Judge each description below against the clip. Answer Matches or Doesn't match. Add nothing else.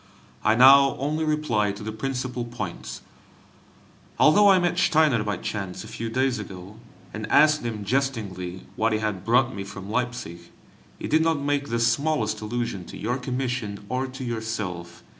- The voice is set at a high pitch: Doesn't match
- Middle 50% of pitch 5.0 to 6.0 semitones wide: Doesn't match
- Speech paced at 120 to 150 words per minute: Doesn't match